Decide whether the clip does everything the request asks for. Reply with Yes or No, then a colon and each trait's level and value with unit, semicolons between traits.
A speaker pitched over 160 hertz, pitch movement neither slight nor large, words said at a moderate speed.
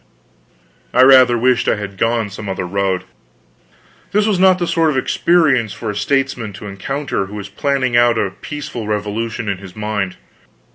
No: low, 115 Hz; average, 5.0 semitones; average, 175 wpm